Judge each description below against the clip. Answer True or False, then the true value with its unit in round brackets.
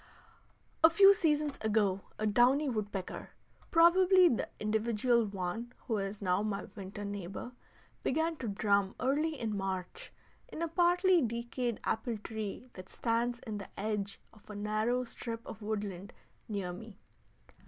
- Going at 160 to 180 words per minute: False (145 wpm)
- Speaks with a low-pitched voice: False (220 Hz)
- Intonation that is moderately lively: True (4.2 semitones)